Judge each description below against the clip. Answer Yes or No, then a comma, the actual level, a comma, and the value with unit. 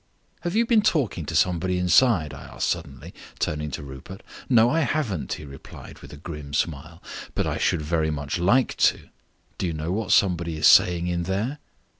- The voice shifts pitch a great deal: Yes, wide, 5.8 semitones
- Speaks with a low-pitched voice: Yes, very low, 85 Hz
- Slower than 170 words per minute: No, average, 190 wpm